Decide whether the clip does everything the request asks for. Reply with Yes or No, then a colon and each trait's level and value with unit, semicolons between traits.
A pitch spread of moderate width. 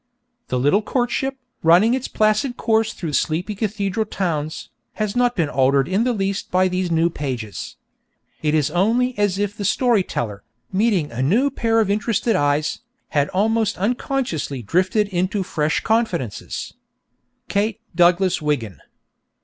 No: wide, 6.2 semitones